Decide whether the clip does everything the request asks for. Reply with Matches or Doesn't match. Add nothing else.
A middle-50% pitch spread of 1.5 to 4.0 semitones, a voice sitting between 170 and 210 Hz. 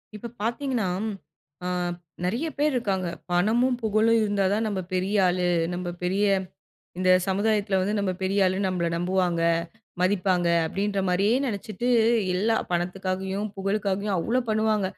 Matches